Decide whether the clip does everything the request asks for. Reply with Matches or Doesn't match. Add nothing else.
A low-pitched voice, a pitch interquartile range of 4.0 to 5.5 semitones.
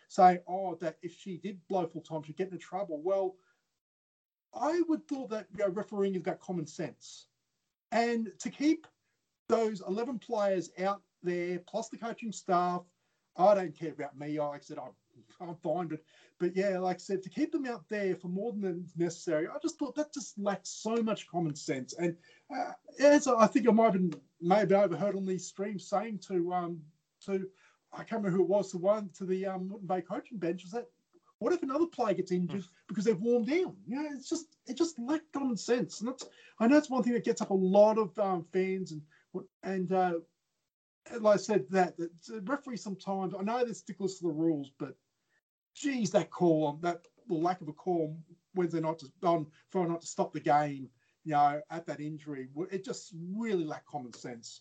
Doesn't match